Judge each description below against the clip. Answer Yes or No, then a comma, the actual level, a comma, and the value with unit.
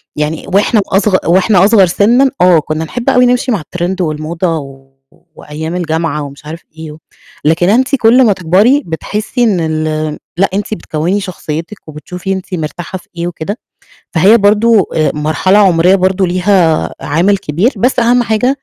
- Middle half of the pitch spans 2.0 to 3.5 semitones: No, average, 4.7 semitones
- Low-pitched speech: No, medium, 185 Hz